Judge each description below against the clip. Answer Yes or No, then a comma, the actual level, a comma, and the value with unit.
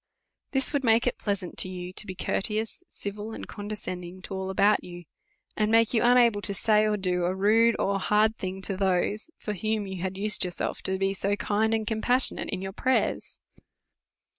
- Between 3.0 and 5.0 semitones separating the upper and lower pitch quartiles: No, narrow, 2.6 semitones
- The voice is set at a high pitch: Yes, high, 205 Hz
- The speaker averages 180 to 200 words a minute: Yes, average, 195 wpm